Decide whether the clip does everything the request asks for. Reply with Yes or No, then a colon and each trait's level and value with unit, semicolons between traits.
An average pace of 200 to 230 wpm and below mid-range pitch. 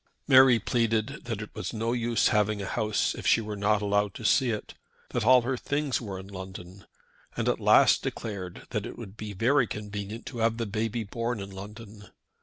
Yes: fast, 205 wpm; low, 110 Hz